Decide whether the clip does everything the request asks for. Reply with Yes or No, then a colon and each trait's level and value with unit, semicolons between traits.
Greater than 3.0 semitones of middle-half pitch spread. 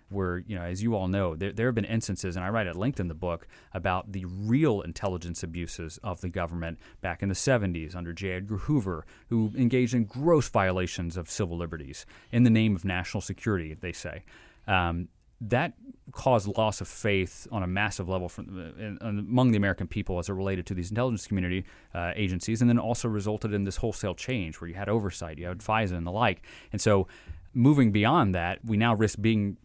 Yes: average, 3.8 semitones